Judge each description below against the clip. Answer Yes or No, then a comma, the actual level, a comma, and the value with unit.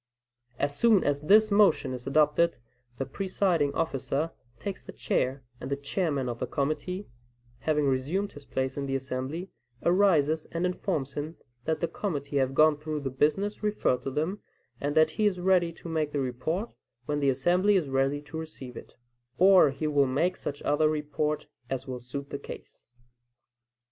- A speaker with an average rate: Yes, average, 175 wpm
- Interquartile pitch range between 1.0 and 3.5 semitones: No, average, 4.2 semitones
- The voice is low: No, medium, 150 Hz